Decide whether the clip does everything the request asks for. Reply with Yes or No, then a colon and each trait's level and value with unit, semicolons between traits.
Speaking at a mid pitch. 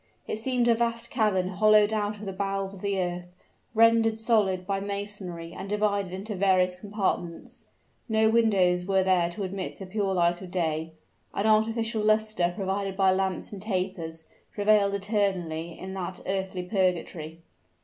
No: high, 195 Hz